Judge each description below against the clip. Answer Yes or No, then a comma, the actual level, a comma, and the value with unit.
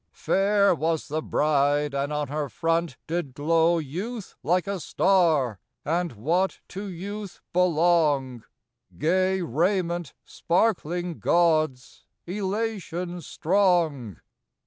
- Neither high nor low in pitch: Yes, medium, 170 Hz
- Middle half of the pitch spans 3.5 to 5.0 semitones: Yes, average, 3.8 semitones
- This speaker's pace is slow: Yes, slow, 100 wpm